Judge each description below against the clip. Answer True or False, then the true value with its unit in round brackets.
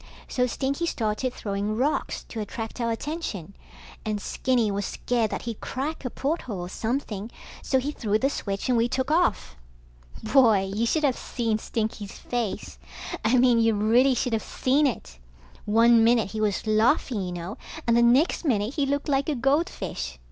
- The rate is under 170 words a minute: False (175 wpm)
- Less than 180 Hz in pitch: False (230 Hz)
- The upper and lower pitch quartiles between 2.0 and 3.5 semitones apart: False (3.9 semitones)